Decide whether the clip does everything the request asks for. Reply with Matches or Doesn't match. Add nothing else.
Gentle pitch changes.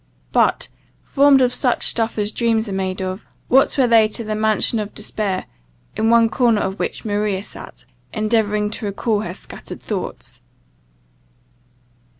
Matches